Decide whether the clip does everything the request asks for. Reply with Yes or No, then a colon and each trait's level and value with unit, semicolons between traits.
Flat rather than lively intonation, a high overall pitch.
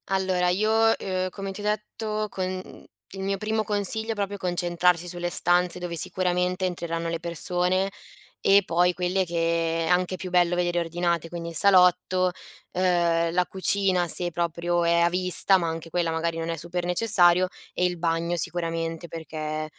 No: narrow, 1.7 semitones; medium, 180 Hz